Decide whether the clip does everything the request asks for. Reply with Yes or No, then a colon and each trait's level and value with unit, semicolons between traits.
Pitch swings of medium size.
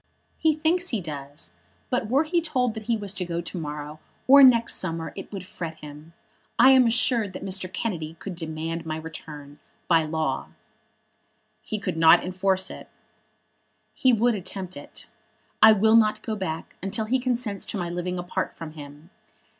No: wide, 5.9 semitones